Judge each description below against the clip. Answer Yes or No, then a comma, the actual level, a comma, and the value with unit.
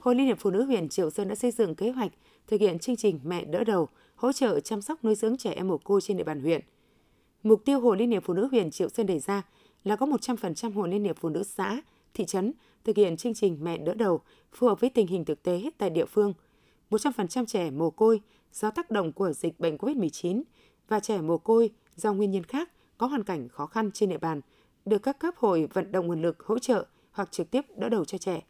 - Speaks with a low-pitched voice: No, high, 205 Hz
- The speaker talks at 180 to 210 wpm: No, fast, 250 wpm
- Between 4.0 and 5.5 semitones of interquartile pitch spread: Yes, average, 4.4 semitones